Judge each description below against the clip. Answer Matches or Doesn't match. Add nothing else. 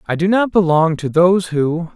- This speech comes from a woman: Doesn't match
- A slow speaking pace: Doesn't match